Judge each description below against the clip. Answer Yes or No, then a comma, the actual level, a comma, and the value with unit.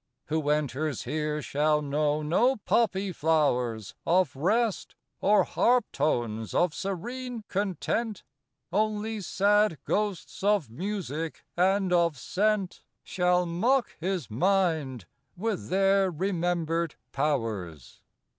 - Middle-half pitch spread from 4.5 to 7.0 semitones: Yes, average, 5.2 semitones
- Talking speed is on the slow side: Yes, slow, 105 wpm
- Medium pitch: Yes, medium, 175 Hz